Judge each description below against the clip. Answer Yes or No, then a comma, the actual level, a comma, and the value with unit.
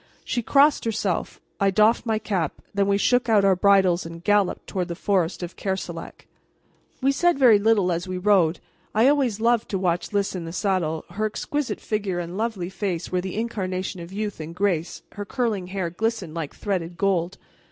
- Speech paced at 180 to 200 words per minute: Yes, average, 190 wpm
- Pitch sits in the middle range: No, high, 195 Hz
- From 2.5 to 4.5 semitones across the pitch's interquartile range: Yes, average, 3.4 semitones